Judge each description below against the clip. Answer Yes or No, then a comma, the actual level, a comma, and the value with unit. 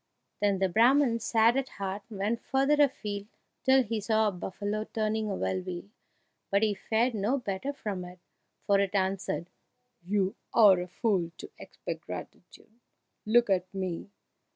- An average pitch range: Yes, average, 3.1 semitones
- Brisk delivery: No, average, 155 wpm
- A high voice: Yes, high, 205 Hz